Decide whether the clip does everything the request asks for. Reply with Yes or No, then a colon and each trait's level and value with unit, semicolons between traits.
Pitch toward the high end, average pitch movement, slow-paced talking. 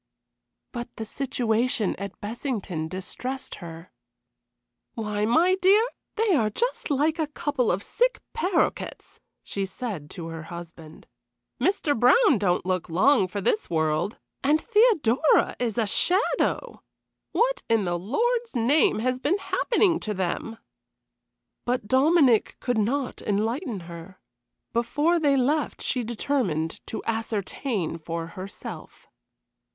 No: high, 235 Hz; wide, 7.7 semitones; slow, 125 wpm